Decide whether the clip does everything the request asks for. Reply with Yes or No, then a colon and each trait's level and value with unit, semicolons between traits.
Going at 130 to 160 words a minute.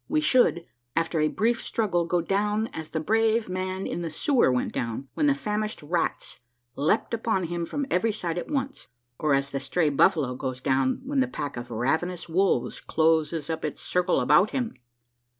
No: average, 185 wpm